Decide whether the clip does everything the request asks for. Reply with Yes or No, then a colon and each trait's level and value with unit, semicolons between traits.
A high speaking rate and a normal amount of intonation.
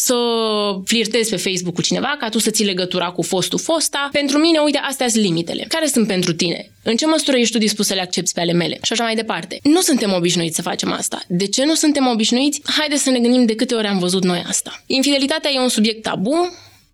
No: fast, 235 wpm; wide, 6.9 semitones